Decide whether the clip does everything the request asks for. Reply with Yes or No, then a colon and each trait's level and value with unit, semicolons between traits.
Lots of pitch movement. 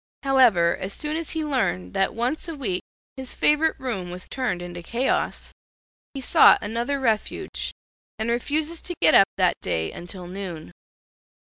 Yes: wide, 7.4 semitones